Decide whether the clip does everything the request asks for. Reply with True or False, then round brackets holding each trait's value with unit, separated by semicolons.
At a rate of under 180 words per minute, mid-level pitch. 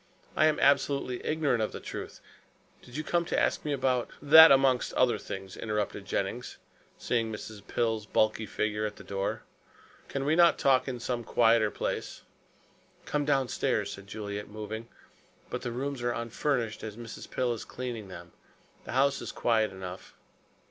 False (170 wpm; 120 Hz)